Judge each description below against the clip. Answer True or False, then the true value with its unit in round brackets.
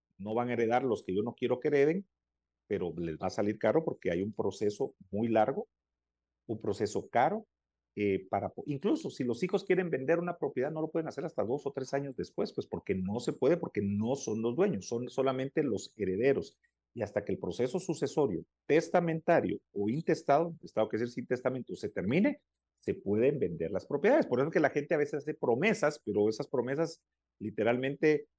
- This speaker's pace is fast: True (205 wpm)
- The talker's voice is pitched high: False (125 Hz)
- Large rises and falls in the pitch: True (7.1 semitones)